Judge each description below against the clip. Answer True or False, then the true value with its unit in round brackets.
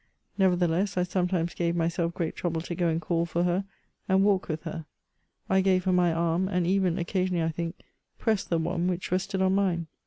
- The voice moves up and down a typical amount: False (1.9 semitones)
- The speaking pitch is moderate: True (175 Hz)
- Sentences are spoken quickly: True (210 wpm)